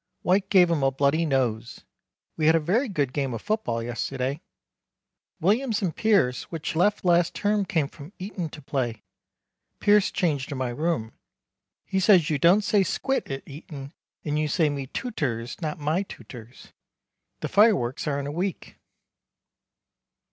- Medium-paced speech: Yes, average, 155 wpm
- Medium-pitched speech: Yes, medium, 155 Hz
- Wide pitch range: Yes, wide, 5.9 semitones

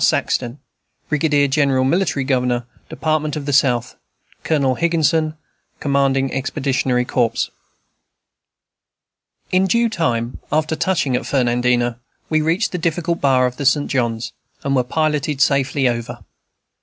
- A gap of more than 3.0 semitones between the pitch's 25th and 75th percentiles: Yes, average, 3.7 semitones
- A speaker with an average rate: No, slow, 125 wpm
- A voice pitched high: No, medium, 140 Hz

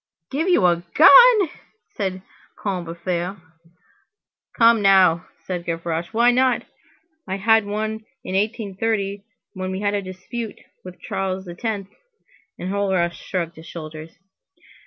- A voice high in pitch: Yes, high, 195 Hz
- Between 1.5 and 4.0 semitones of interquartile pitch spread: Yes, average, 3.6 semitones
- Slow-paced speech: Yes, slow, 115 wpm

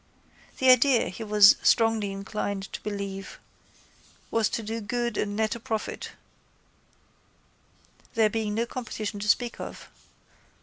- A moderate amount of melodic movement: No, narrow, 2.0 semitones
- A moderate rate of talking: No, slow, 130 wpm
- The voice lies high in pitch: Yes, high, 215 Hz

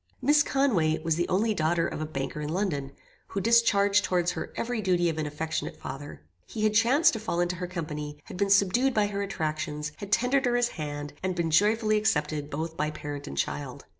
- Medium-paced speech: No, fast, 210 wpm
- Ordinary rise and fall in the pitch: No, wide, 5.7 semitones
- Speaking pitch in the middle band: Yes, medium, 175 Hz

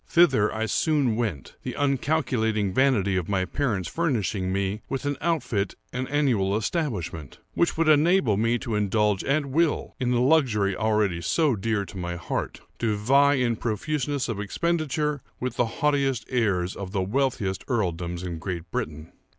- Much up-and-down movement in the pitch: Yes, wide, 6.2 semitones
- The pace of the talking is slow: No, average, 160 wpm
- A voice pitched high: No, low, 115 Hz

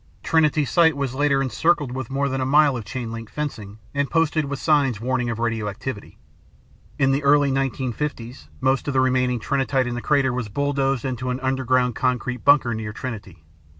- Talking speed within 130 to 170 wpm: No, average, 185 wpm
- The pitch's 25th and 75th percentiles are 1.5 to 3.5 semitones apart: Yes, average, 2.7 semitones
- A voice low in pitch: Yes, low, 130 Hz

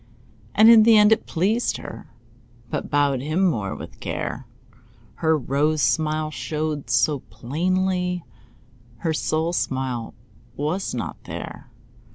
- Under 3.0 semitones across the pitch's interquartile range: No, average, 4.4 semitones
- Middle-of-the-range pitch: Yes, medium, 155 Hz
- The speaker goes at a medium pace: No, slow, 125 wpm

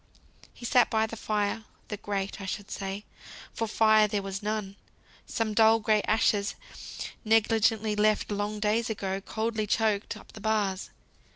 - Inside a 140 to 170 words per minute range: Yes, average, 155 wpm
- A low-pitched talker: No, high, 215 Hz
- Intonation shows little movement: Yes, narrow, 1.4 semitones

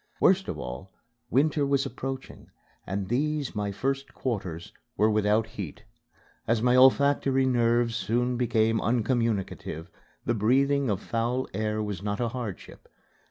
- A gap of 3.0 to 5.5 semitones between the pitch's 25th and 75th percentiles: Yes, average, 4.0 semitones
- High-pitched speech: No, low, 115 Hz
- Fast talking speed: No, slow, 135 wpm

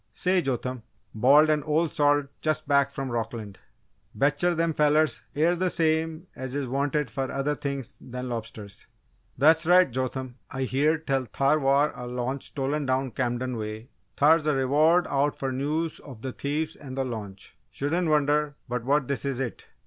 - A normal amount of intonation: Yes, average, 3.0 semitones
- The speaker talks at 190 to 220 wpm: No, average, 170 wpm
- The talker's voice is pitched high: No, medium, 140 Hz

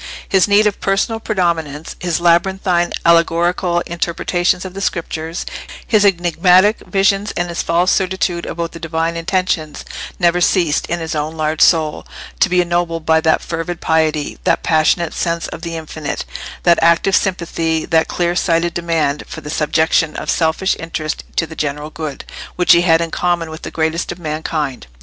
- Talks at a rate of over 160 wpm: Yes, average, 170 wpm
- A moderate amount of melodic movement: No, narrow, 1.8 semitones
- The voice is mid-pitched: Yes, medium, 170 Hz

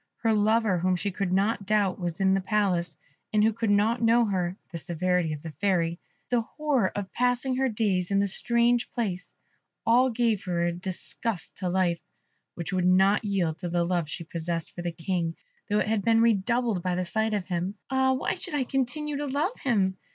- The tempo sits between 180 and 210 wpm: Yes, fast, 205 wpm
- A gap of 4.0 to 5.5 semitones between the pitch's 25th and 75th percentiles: Yes, average, 4.5 semitones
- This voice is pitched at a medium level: No, high, 200 Hz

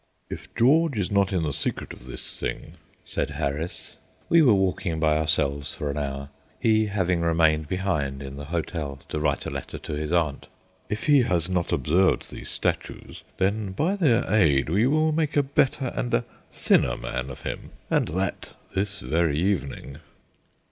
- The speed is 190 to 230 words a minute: No, average, 175 wpm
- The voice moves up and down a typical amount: No, wide, 6.3 semitones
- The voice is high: No, very low, 85 Hz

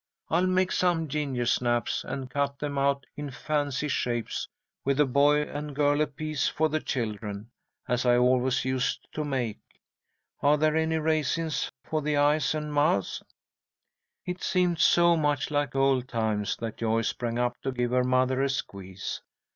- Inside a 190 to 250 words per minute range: No, average, 160 wpm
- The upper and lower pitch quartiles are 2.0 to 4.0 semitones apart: Yes, average, 3.5 semitones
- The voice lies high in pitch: No, medium, 140 Hz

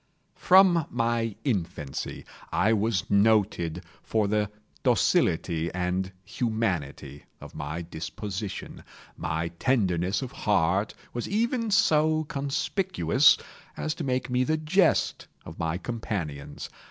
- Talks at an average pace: No, slow, 110 wpm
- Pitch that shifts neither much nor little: No, wide, 8.0 semitones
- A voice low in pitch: Yes, low, 105 Hz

